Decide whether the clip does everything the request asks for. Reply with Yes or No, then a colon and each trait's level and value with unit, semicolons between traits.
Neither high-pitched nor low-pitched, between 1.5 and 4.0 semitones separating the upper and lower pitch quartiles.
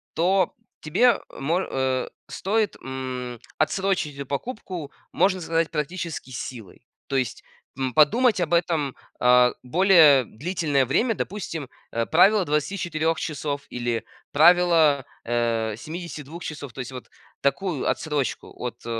No: medium, 150 Hz; average, 5.1 semitones